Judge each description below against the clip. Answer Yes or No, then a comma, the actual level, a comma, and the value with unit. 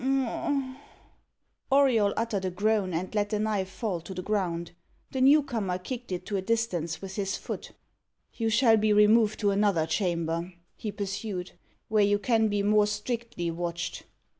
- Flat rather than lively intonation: No, average, 3.2 semitones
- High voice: Yes, high, 205 Hz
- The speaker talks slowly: No, average, 165 wpm